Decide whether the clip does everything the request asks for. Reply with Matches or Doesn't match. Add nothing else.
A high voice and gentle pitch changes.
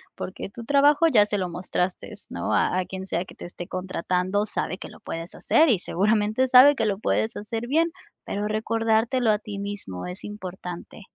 Doesn't match